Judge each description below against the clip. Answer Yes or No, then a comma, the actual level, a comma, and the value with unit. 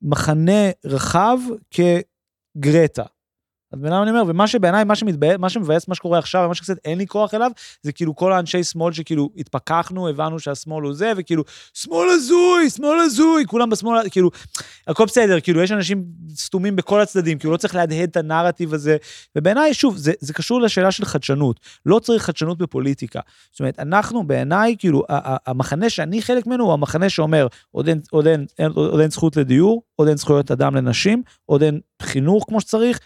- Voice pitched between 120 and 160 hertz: No, medium, 175 Hz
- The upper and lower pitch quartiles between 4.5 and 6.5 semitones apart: Yes, wide, 5.4 semitones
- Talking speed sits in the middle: No, fast, 160 wpm